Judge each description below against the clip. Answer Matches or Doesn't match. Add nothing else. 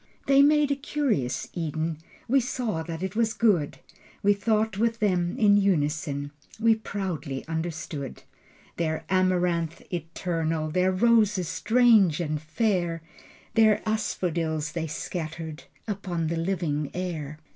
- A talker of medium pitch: Matches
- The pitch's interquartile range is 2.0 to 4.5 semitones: Doesn't match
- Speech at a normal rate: Doesn't match